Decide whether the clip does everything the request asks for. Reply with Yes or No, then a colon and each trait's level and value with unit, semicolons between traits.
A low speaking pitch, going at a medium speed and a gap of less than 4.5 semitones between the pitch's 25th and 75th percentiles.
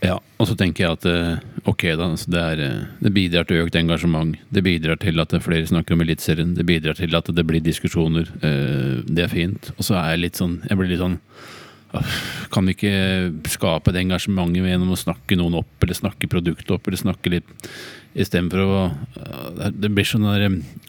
Yes: very low, 90 Hz; average, 195 wpm; narrow, 2.4 semitones